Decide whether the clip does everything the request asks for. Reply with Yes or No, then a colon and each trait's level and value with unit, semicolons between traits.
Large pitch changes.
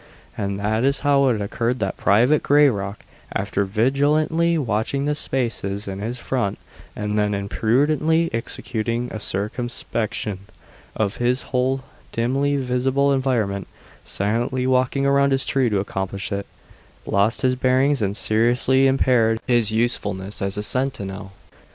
No: average, 4.5 semitones